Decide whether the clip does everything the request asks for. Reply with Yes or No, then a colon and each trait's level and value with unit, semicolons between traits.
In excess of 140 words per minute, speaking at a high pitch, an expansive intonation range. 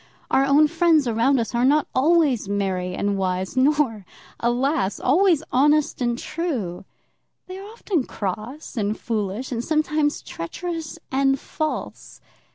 No: slow, 135 wpm; very high, 265 Hz; wide, 6.0 semitones